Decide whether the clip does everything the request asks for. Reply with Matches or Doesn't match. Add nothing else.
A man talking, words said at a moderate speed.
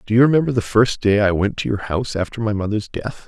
Doesn't match